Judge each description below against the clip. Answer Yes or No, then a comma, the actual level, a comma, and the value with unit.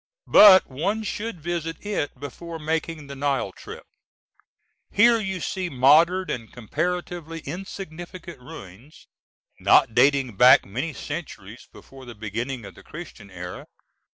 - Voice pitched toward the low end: No, medium, 150 Hz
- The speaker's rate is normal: No, slow, 125 wpm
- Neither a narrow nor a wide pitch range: No, wide, 5.9 semitones